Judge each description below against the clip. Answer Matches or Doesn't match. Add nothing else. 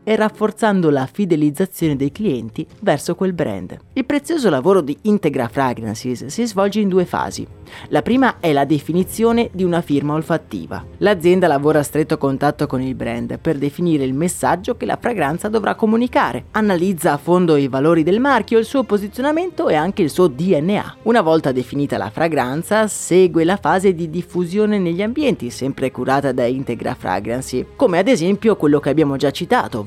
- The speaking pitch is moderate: Matches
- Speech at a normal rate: Doesn't match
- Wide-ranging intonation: Matches